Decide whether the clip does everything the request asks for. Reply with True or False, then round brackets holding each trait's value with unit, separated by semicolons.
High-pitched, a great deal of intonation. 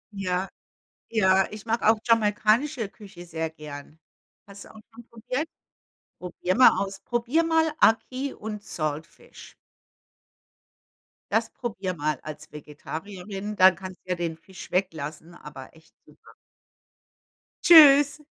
True (195 Hz; 5.7 semitones)